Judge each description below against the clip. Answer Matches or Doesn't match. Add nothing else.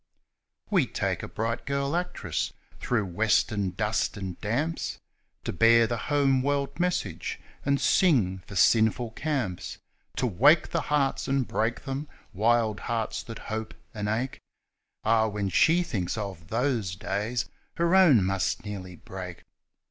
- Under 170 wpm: Matches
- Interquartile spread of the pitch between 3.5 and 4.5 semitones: Doesn't match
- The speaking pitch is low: Matches